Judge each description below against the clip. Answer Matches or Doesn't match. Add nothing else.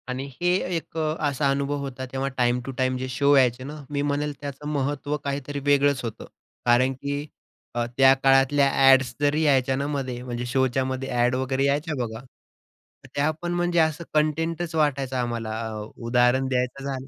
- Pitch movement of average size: Doesn't match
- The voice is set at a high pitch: Doesn't match